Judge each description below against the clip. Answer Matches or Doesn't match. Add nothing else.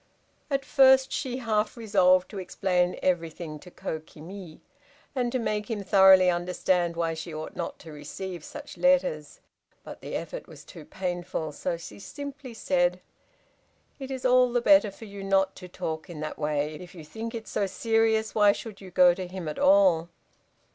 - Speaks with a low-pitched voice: Doesn't match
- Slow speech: Doesn't match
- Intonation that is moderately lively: Matches